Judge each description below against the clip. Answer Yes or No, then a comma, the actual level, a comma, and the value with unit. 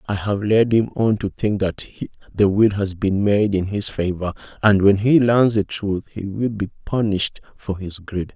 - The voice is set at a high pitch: No, low, 100 Hz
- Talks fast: Yes, fast, 210 wpm